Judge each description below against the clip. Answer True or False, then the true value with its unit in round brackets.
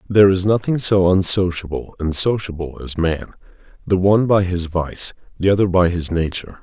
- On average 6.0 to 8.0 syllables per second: False (5.3 syllables/s)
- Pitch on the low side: True (90 Hz)